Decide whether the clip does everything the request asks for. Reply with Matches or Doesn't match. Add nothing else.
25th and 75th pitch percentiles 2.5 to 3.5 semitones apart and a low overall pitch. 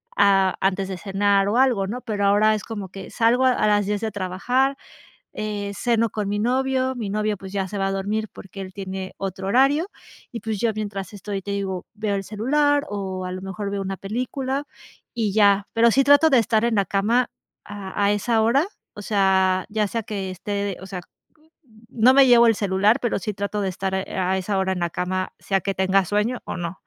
Doesn't match